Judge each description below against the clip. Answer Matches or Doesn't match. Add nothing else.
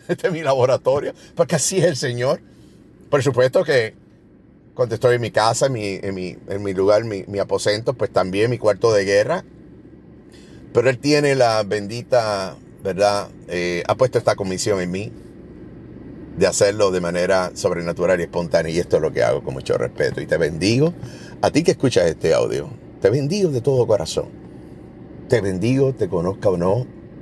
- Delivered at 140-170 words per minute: Doesn't match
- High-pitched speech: Doesn't match